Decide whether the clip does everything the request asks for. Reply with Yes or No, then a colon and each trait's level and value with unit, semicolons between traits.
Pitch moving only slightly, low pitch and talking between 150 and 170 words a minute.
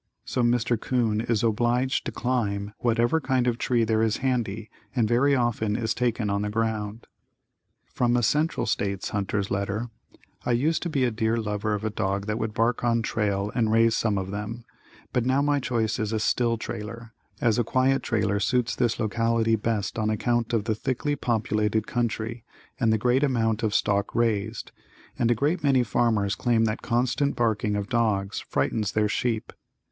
No: narrow, 2.3 semitones; low, 115 Hz; average, 185 wpm